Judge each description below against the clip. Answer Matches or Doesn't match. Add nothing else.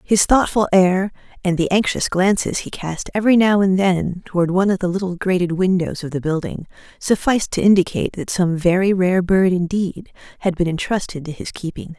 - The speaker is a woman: Matches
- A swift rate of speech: Doesn't match